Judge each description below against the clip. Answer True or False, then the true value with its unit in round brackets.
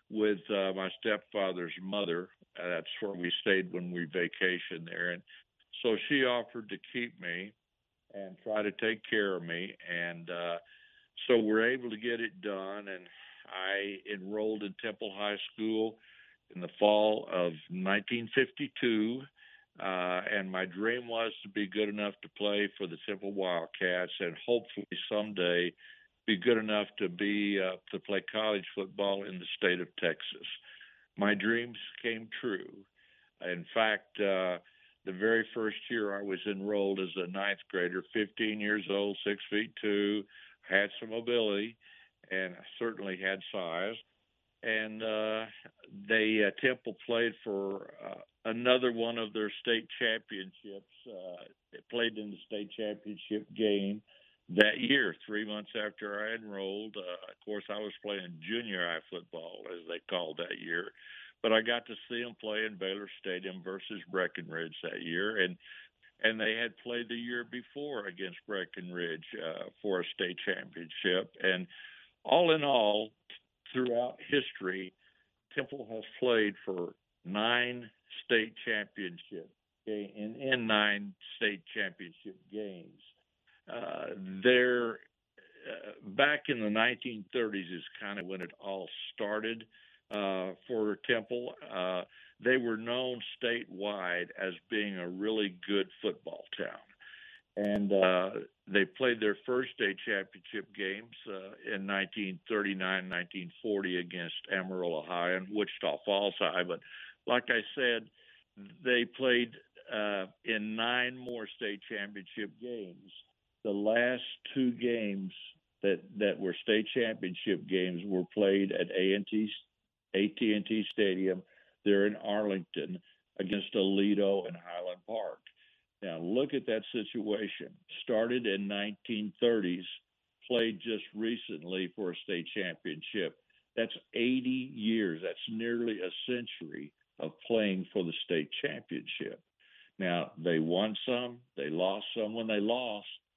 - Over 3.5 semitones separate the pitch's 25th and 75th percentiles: False (3.1 semitones)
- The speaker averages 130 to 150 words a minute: True (140 wpm)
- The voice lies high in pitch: False (105 Hz)